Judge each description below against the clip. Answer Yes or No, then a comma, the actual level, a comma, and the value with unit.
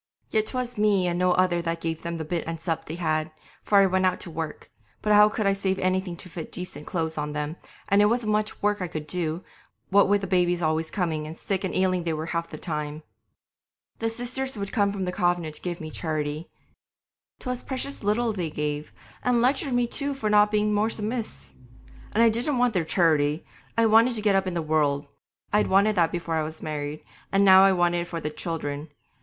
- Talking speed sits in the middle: No, fast, 225 wpm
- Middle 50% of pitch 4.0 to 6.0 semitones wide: Yes, average, 4.6 semitones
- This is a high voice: No, medium, 180 Hz